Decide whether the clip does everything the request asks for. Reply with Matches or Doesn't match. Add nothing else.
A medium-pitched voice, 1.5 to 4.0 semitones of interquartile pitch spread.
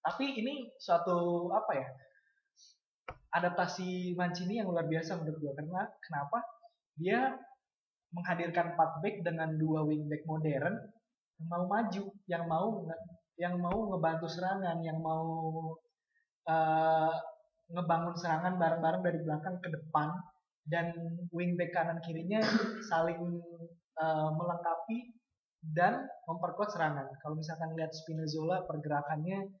Matches